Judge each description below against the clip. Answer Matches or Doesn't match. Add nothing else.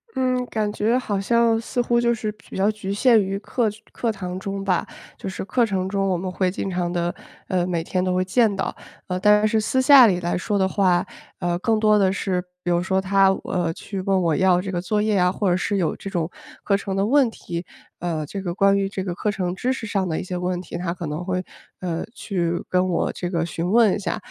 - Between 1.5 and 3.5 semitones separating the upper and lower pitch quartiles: Matches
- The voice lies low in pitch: Doesn't match